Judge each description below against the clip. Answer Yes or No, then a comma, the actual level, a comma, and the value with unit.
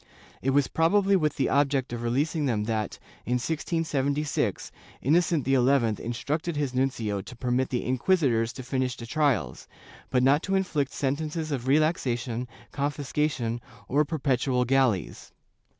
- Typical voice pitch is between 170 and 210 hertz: No, low, 135 Hz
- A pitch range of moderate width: Yes, average, 3.6 semitones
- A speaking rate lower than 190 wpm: Yes, average, 140 wpm